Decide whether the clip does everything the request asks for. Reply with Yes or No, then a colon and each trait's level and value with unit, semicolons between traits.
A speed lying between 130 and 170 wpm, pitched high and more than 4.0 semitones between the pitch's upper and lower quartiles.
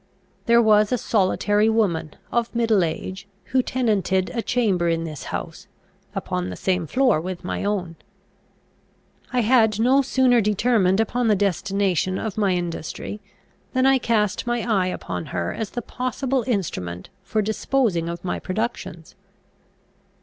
Yes: average, 145 wpm; high, 210 Hz; average, 4.5 semitones